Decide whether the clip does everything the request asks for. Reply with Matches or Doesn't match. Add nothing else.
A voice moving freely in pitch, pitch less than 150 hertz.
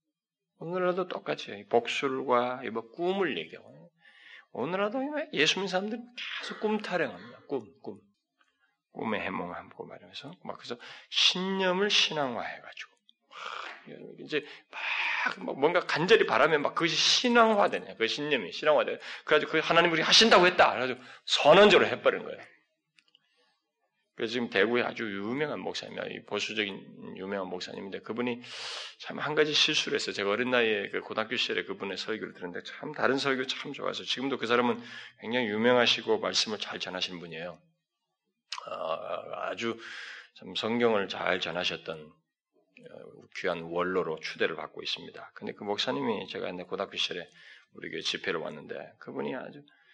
Matches